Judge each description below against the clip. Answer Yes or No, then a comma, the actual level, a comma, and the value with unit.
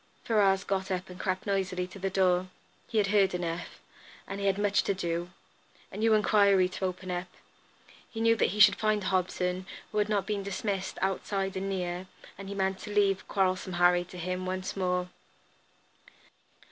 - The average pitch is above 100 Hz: Yes, high, 190 Hz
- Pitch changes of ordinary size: No, narrow, 1.6 semitones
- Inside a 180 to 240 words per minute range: Yes, average, 185 wpm